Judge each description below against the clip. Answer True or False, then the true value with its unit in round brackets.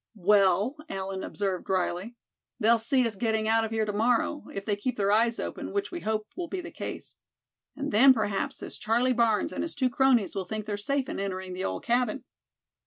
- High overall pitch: True (220 Hz)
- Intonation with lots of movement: False (3.9 semitones)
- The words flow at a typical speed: False (210 wpm)